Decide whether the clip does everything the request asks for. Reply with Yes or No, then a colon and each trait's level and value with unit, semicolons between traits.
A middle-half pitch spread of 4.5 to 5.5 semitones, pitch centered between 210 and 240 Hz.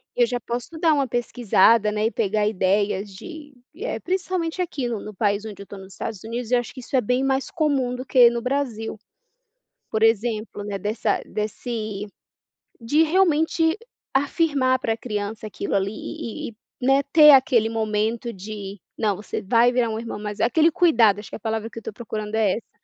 No: average, 4.1 semitones; high, 230 Hz